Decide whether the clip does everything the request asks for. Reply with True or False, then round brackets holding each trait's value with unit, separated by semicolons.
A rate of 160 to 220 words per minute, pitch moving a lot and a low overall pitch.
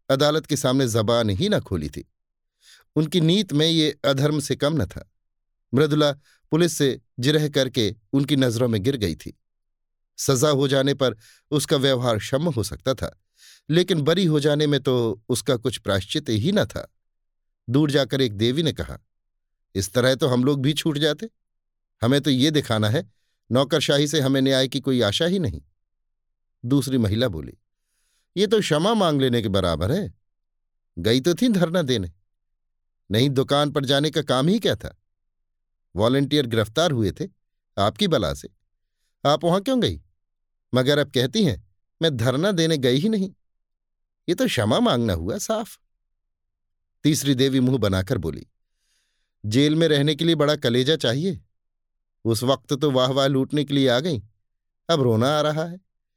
True (170 wpm; 6.7 semitones; 130 Hz)